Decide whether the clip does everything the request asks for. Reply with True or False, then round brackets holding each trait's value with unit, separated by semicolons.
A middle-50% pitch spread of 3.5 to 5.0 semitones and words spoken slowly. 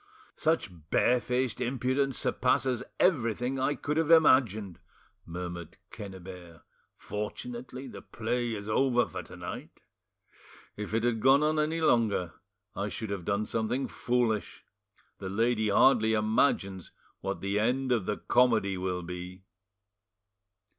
True (4.5 semitones; 125 wpm)